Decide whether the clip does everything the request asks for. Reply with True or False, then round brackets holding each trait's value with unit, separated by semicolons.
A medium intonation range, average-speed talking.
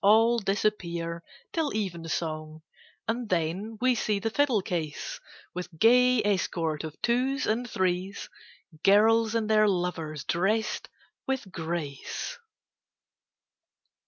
False (5.0 semitones; 105 wpm)